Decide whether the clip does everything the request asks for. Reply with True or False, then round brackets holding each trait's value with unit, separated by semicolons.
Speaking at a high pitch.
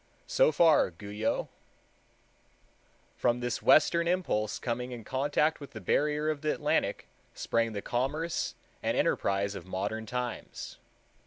False (125 Hz)